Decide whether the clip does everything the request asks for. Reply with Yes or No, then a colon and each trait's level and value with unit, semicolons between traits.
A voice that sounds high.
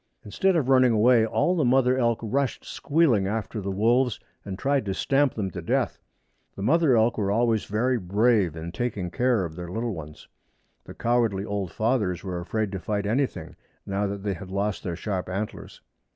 No: low, 110 Hz